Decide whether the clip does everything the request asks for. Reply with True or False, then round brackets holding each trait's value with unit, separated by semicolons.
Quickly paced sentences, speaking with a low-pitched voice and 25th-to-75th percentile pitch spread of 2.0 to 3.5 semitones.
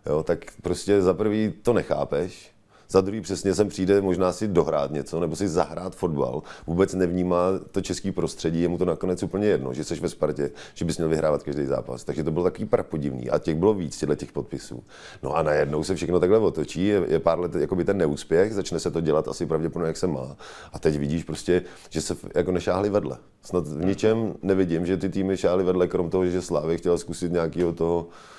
True (215 wpm; 90 Hz; 2.6 semitones)